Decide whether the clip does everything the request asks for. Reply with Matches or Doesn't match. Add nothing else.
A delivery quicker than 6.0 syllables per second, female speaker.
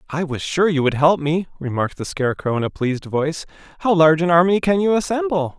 Doesn't match